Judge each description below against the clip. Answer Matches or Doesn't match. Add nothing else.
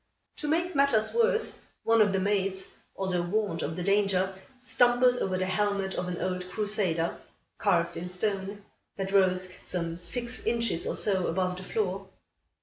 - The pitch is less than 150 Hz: Doesn't match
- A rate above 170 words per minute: Doesn't match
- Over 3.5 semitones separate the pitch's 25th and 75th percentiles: Doesn't match